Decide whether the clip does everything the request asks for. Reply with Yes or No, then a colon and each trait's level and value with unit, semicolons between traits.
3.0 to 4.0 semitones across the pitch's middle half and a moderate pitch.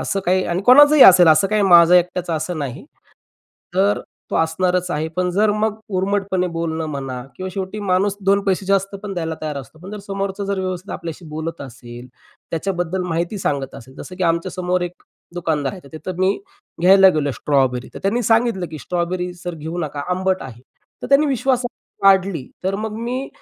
Yes: average, 3.5 semitones; medium, 180 Hz